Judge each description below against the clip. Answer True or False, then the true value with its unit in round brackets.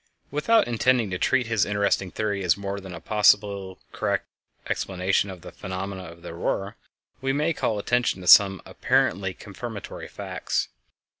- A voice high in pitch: False (100 Hz)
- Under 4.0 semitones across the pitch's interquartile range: True (3.3 semitones)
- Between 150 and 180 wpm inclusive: True (155 wpm)